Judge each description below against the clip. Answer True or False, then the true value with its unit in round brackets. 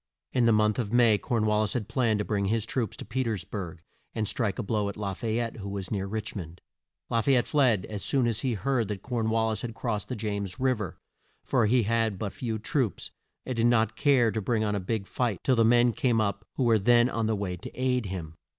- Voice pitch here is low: True (110 Hz)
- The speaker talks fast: True (260 wpm)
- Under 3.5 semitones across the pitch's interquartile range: True (2.8 semitones)